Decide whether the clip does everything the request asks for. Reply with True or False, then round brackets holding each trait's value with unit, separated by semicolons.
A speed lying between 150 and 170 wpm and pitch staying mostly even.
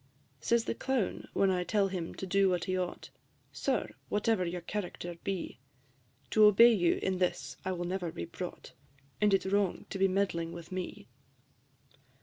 False (180 wpm; 2.3 semitones)